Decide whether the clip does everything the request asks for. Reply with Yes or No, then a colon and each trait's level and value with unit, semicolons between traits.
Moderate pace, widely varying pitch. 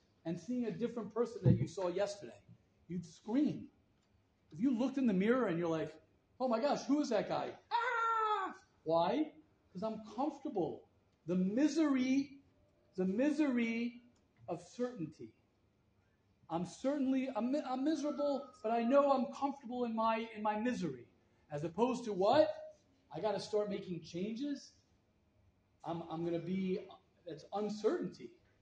Yes: average, 145 wpm; wide, 8.2 semitones